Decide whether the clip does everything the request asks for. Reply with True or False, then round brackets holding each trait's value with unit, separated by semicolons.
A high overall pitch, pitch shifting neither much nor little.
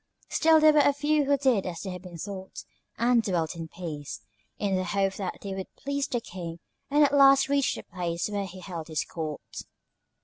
False (195 Hz; 7.8 semitones)